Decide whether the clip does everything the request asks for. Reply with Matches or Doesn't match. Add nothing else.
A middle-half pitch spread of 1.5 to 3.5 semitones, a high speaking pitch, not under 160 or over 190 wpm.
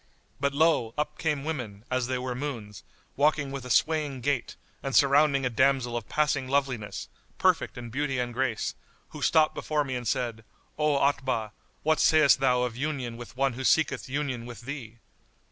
Doesn't match